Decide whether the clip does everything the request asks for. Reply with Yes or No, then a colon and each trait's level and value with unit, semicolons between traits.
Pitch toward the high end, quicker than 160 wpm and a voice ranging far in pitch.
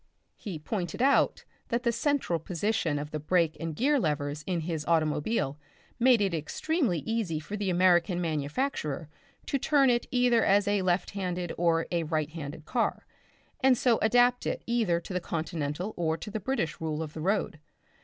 No: medium, 175 Hz; average, 180 wpm; wide, 6.5 semitones